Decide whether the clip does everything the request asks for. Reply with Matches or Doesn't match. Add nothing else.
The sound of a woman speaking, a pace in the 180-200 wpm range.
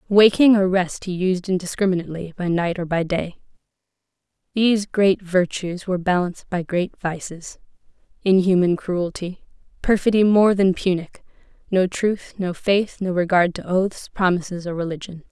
Doesn't match